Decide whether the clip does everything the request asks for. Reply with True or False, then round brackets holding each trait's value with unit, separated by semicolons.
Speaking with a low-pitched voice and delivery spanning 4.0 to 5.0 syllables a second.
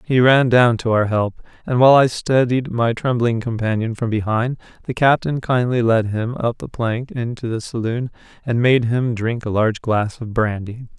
True (120 Hz; 4.7 syllables/s)